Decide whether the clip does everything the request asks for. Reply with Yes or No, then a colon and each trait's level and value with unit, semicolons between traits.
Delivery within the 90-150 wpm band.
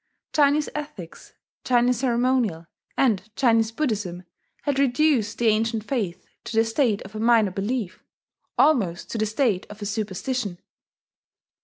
Yes: slow, 135 wpm